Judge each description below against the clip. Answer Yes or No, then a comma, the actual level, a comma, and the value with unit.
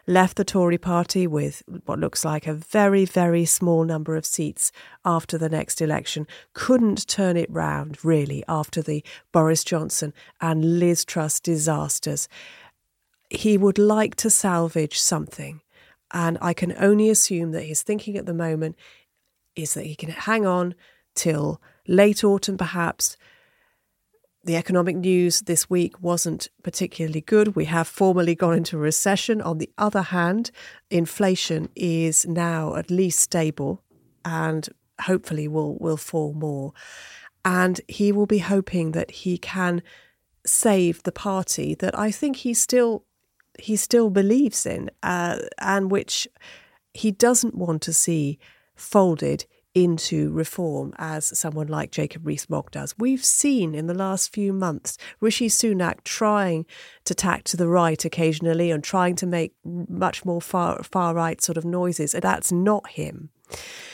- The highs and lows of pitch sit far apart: No, average, 3.7 semitones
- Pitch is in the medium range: Yes, medium, 175 Hz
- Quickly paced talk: No, average, 150 wpm